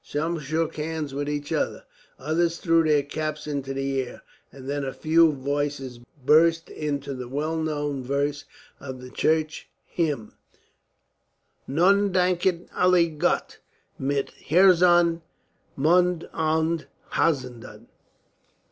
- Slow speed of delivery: Yes, slow, 120 wpm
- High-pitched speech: No, medium, 155 Hz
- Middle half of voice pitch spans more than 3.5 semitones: No, average, 2.9 semitones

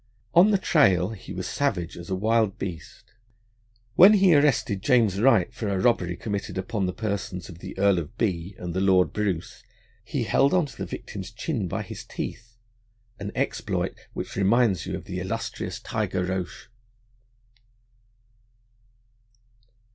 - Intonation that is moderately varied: Yes, average, 4.1 semitones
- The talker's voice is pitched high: No, low, 100 Hz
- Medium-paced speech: Yes, average, 160 wpm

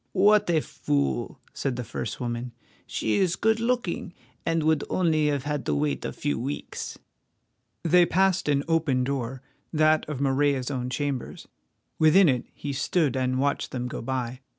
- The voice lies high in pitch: No, medium, 145 Hz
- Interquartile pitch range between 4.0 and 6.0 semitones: Yes, average, 4.4 semitones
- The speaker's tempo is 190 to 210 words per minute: No, average, 165 wpm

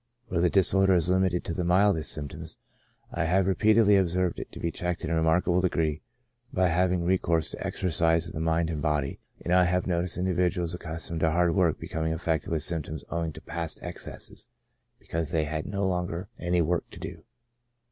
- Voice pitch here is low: Yes, very low, 85 Hz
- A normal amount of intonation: No, narrow, 2.0 semitones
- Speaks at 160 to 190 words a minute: No, average, 200 wpm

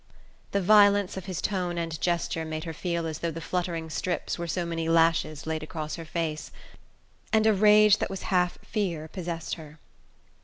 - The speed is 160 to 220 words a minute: Yes, average, 185 wpm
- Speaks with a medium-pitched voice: Yes, medium, 170 Hz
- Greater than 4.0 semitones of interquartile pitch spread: No, narrow, 2.6 semitones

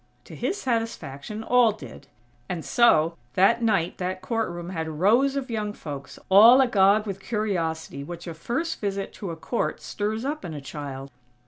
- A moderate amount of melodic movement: No, wide, 5.9 semitones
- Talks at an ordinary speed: Yes, average, 175 wpm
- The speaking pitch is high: Yes, high, 195 Hz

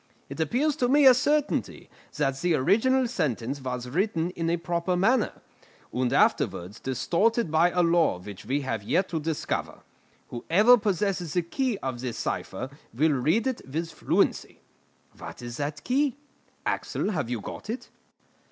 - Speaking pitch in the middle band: Yes, medium, 170 Hz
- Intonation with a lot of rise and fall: Yes, wide, 8.9 semitones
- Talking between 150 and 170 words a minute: Yes, average, 160 wpm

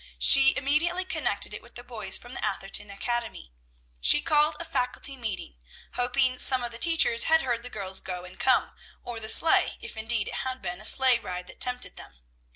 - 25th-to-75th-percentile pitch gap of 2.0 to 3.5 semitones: No, average, 4.2 semitones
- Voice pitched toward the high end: Yes, high, 245 Hz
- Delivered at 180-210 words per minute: Yes, average, 200 wpm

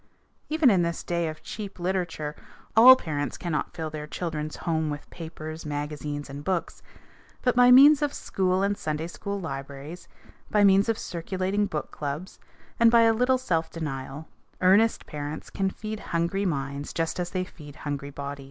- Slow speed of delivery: No, average, 170 wpm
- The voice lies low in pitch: No, medium, 170 Hz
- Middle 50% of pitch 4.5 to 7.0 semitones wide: Yes, average, 5.1 semitones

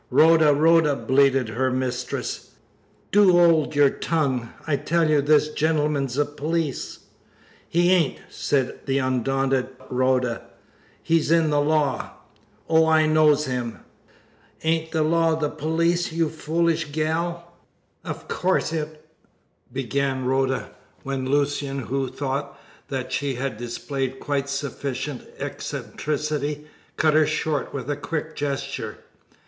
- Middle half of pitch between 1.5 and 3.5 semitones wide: Yes, average, 2.9 semitones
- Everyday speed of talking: No, slow, 125 wpm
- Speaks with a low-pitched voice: No, medium, 145 Hz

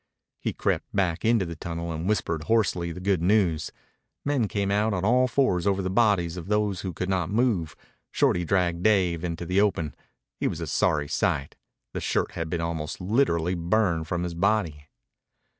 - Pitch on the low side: Yes, very low, 90 Hz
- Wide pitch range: No, average, 3.7 semitones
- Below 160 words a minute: No, average, 185 wpm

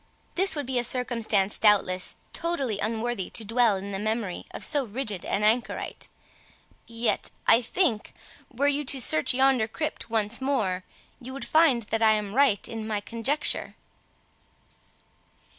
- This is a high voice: Yes, high, 230 Hz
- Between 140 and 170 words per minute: Yes, average, 150 wpm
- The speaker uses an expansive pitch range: No, average, 4.1 semitones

